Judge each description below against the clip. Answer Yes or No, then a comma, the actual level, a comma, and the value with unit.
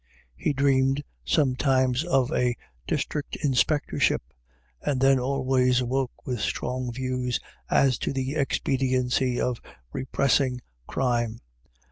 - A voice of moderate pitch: No, low, 130 Hz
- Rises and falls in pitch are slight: Yes, narrow, 1.3 semitones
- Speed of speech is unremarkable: No, slow, 105 wpm